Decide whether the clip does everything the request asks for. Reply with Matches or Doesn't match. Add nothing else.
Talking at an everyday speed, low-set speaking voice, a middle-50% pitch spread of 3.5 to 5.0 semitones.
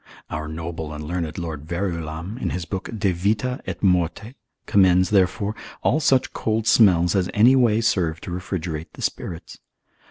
Matches